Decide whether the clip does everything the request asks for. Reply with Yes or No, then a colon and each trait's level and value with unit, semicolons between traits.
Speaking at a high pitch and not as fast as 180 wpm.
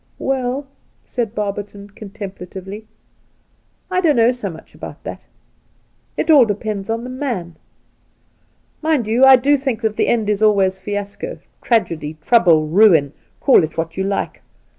Yes: high, 210 Hz; average, 155 wpm